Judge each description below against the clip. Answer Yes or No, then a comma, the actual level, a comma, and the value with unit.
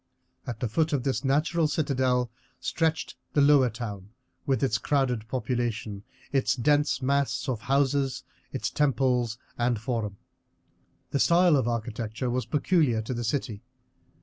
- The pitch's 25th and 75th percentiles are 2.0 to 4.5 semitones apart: Yes, average, 3.4 semitones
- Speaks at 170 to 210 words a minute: No, average, 140 wpm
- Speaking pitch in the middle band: No, low, 130 Hz